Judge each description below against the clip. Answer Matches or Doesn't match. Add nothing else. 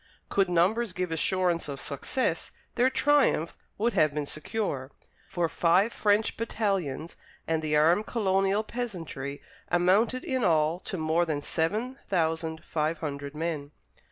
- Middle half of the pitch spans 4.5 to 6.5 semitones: Matches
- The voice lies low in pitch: Doesn't match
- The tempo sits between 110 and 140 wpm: Matches